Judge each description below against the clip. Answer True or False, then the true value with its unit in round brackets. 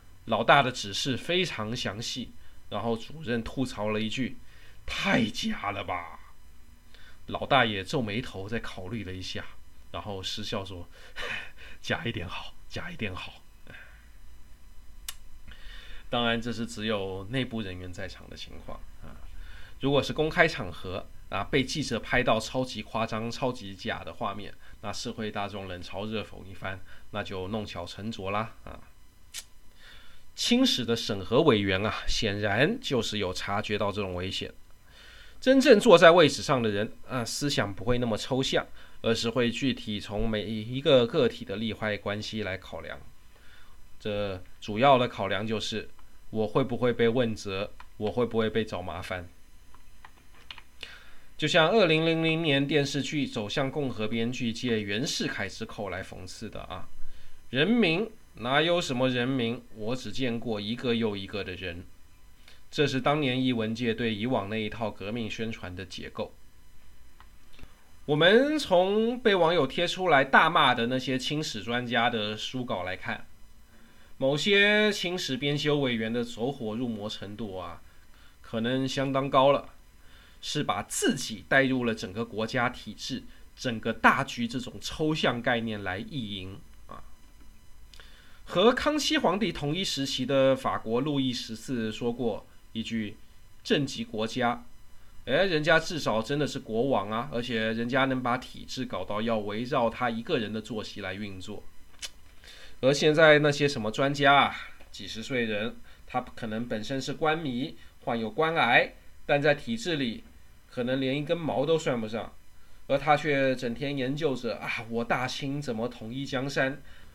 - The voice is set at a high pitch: False (115 Hz)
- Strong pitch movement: False (4.9 semitones)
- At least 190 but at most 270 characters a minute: True (225 characters per minute)